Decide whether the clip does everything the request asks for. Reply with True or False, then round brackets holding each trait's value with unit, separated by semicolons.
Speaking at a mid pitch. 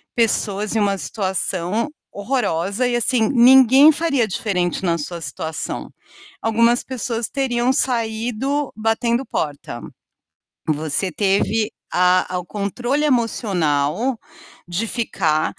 False (220 Hz)